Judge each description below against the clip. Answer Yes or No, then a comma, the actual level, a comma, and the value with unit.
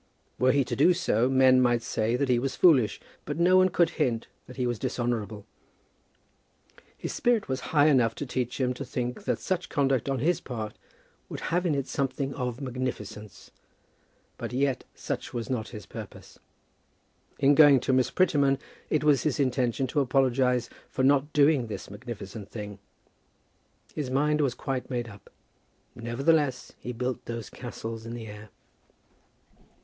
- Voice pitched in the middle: No, low, 130 Hz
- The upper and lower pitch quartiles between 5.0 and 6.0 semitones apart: No, average, 3.1 semitones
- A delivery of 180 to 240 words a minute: No, average, 165 wpm